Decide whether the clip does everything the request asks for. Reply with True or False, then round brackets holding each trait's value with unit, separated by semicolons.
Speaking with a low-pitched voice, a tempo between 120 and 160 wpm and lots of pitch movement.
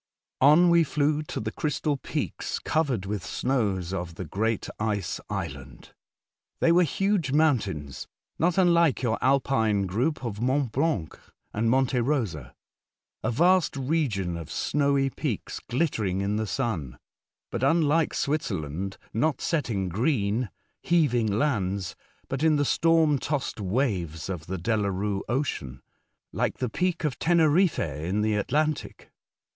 True (125 Hz; 140 wpm; 7.4 semitones)